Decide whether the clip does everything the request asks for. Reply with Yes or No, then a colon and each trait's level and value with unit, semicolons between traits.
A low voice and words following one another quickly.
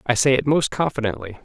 Yes: low, 130 Hz; fast, 210 wpm